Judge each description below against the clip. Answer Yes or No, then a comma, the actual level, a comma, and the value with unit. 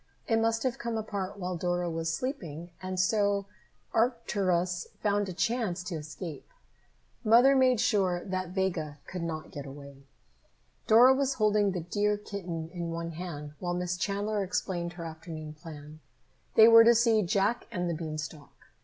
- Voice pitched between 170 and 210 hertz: Yes, medium, 185 Hz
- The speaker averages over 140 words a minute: Yes, average, 160 wpm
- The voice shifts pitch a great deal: No, average, 4.3 semitones